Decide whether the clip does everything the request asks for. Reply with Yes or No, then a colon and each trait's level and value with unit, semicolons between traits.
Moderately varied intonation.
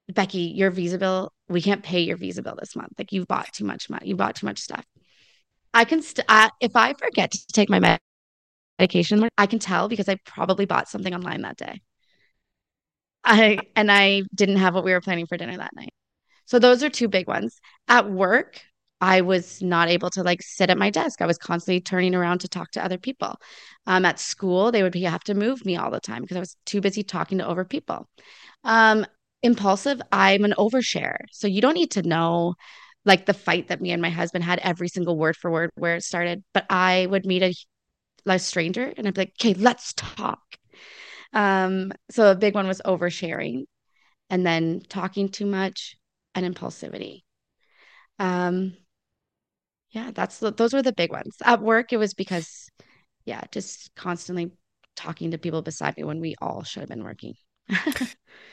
Yes: average, 3.2 semitones